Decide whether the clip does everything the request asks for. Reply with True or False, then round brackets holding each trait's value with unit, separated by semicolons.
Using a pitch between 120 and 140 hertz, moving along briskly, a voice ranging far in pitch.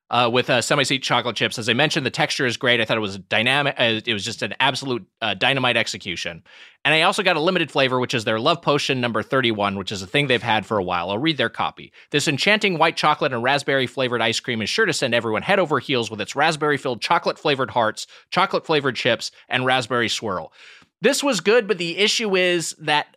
False (135 Hz; 240 wpm; 5.0 semitones)